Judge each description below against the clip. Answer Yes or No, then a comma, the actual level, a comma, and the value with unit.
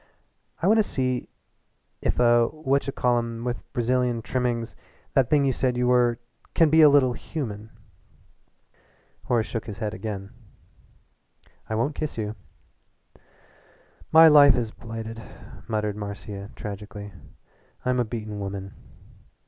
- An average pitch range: Yes, average, 3.3 semitones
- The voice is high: No, low, 120 Hz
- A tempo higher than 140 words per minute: No, slow, 135 wpm